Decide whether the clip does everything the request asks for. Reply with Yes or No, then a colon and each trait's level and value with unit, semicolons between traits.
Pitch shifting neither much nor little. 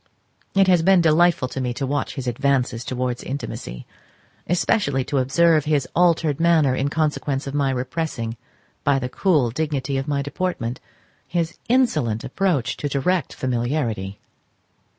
Yes: average, 4.3 semitones